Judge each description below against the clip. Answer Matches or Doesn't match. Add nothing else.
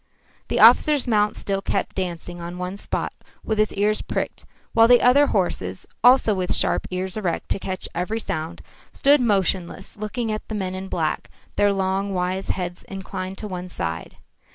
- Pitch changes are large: Doesn't match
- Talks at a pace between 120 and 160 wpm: Doesn't match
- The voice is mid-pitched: Doesn't match